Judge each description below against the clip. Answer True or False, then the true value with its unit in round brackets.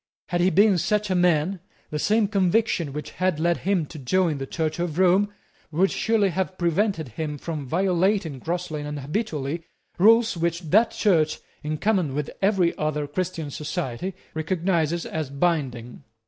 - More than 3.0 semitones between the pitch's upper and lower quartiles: True (3.9 semitones)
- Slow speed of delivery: False (160 wpm)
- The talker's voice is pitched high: False (170 Hz)